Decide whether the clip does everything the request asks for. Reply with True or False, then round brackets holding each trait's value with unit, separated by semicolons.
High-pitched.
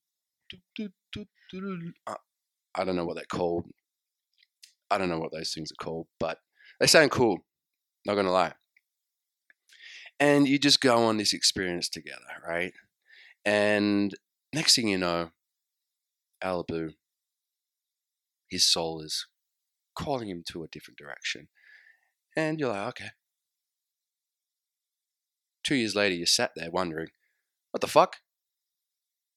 False (100 Hz)